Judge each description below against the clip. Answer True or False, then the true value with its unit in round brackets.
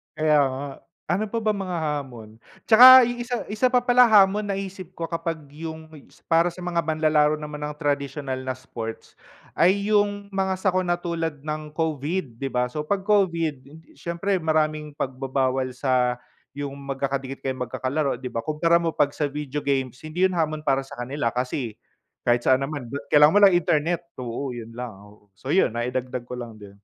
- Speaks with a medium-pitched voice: True (150 Hz)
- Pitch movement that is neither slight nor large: True (5.0 semitones)